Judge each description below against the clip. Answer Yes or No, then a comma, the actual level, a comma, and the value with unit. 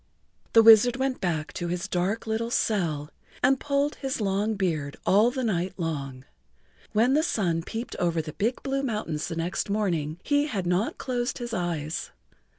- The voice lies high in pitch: Yes, high, 200 Hz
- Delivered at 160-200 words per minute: Yes, average, 170 wpm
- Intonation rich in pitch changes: Yes, wide, 6.1 semitones